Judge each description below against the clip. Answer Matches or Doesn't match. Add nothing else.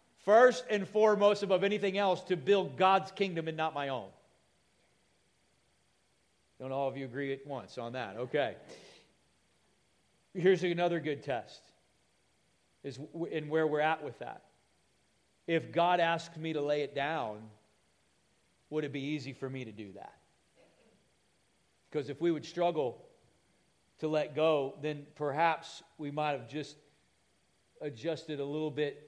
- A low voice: Doesn't match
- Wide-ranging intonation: Doesn't match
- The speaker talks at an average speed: Matches